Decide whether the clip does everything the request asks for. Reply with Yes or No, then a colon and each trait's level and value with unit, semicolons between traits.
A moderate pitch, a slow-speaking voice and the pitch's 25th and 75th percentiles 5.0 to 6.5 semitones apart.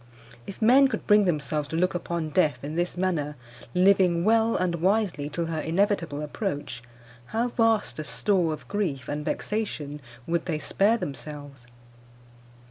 No: medium, 170 Hz; average, 150 wpm; wide, 5.4 semitones